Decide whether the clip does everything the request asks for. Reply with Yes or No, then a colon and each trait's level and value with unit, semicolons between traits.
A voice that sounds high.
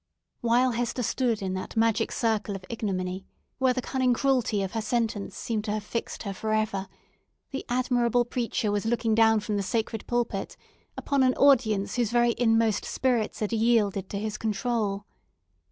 Yes: high, 225 Hz